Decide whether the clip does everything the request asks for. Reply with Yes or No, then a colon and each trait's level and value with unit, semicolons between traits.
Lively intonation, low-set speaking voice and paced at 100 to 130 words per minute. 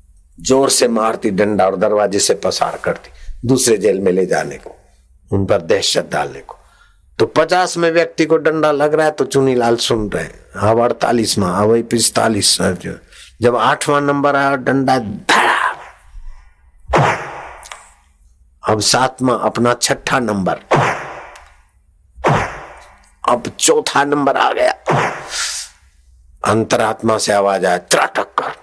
Yes: wide, 8.2 semitones; low, 110 Hz; average, 125 wpm